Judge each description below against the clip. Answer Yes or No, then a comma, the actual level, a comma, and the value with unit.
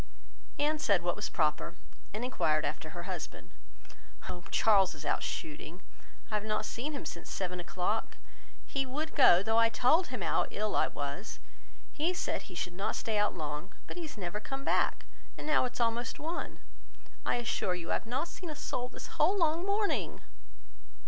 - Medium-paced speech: Yes, average, 190 wpm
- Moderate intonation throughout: No, wide, 8.3 semitones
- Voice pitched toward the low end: No, high, 215 Hz